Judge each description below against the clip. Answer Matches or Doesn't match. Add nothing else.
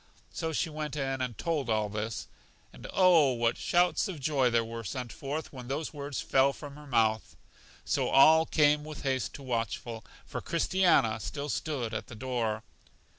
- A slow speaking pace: Doesn't match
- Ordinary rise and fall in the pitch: Matches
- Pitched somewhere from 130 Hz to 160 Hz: Matches